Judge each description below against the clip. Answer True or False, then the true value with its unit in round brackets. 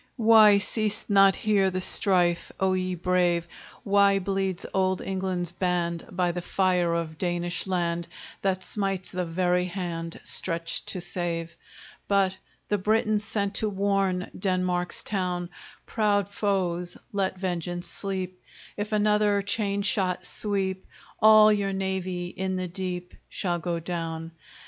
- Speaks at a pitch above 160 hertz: True (185 Hz)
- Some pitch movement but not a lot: False (2.0 semitones)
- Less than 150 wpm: True (135 wpm)